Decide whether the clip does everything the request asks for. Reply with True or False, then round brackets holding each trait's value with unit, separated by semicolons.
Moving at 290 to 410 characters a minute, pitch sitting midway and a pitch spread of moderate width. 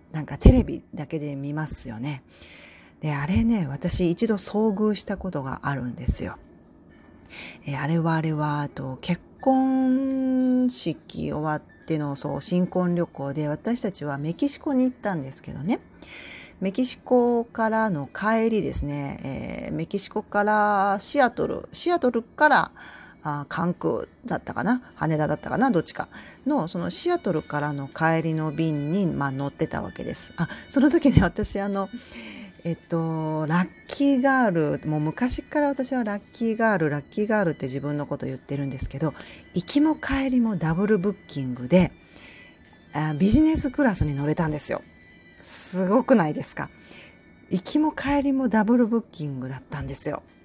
False (320 characters per minute; 175 Hz; 7.9 semitones)